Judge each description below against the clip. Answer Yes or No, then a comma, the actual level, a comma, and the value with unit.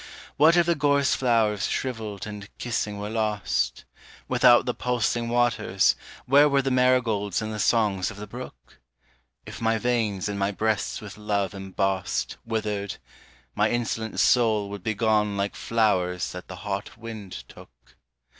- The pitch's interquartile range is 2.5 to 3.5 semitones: Yes, average, 2.9 semitones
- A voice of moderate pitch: No, low, 110 Hz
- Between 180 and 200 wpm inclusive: No, average, 155 wpm